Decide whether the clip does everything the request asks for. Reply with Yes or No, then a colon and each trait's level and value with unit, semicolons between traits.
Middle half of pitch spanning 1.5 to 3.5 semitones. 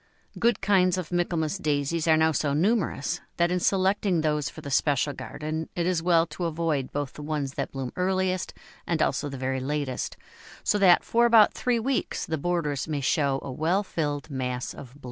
No: average, 4.1 semitones